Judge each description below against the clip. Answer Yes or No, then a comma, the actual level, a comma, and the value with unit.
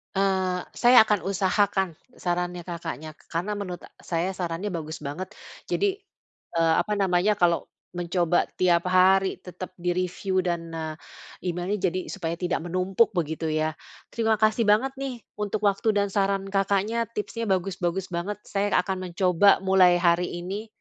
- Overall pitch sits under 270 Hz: Yes, medium, 185 Hz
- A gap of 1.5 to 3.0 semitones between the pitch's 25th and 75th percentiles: Yes, narrow, 2.5 semitones